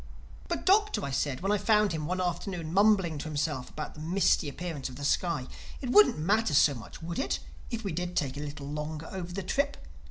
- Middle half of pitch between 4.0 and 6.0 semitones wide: Yes, average, 4.8 semitones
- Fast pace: Yes, fast, 220 wpm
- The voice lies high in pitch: No, medium, 170 Hz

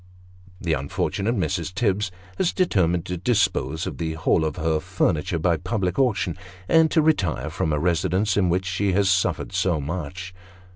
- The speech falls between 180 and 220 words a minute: No, average, 165 wpm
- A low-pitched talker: Yes, very low, 90 Hz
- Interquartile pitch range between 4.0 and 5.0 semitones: No, average, 3.4 semitones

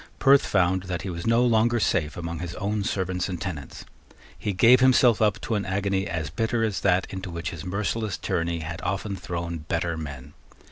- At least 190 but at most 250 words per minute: Yes, average, 195 wpm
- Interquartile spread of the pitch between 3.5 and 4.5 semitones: Yes, average, 4.0 semitones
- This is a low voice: Yes, very low, 95 Hz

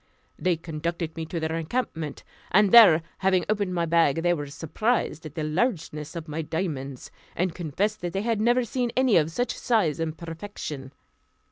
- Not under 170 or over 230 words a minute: Yes, average, 175 wpm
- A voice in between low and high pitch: Yes, medium, 170 Hz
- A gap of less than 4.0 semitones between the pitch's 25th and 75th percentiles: No, average, 4.6 semitones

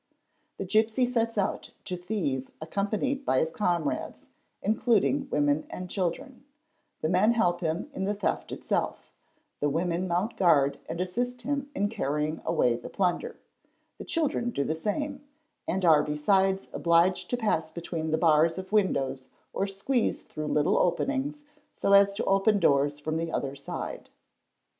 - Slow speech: No, average, 155 wpm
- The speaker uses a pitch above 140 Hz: Yes, medium, 185 Hz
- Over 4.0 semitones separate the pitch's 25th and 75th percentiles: Yes, wide, 5.6 semitones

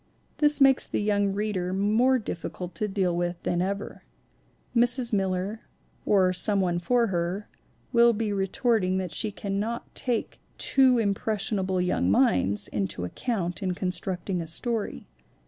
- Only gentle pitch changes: No, average, 3.8 semitones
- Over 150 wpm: No, average, 145 wpm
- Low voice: No, high, 195 Hz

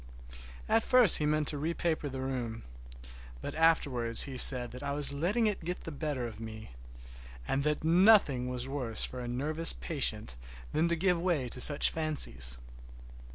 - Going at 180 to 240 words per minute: No, average, 170 wpm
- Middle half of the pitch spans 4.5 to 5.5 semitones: Yes, average, 4.9 semitones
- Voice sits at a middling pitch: Yes, medium, 145 Hz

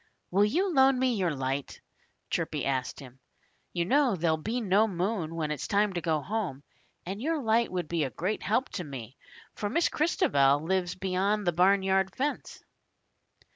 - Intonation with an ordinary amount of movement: No, wide, 5.8 semitones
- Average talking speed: Yes, average, 175 wpm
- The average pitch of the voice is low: No, high, 190 Hz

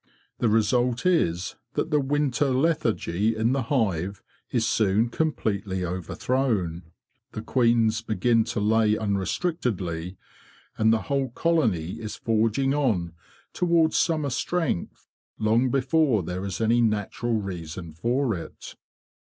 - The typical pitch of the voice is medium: No, low, 115 Hz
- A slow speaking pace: Yes, slow, 120 wpm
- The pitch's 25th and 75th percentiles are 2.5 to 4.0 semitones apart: No, wide, 5.4 semitones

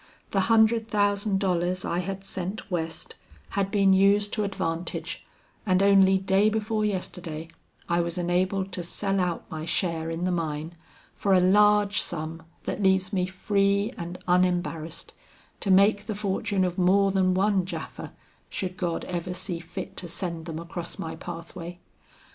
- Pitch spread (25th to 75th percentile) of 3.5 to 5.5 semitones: No, narrow, 2.4 semitones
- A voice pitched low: No, medium, 185 Hz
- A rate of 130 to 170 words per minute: Yes, average, 160 wpm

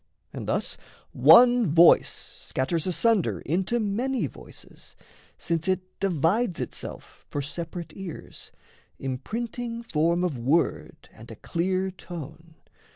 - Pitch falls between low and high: Yes, medium, 180 Hz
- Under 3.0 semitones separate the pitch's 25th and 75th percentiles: No, average, 4.7 semitones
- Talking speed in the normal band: No, slow, 110 wpm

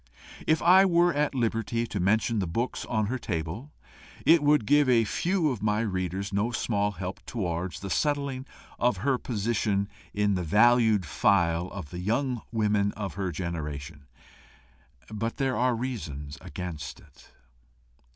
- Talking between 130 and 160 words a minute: Yes, average, 150 wpm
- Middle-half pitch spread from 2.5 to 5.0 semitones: No, wide, 5.4 semitones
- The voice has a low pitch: Yes, low, 105 Hz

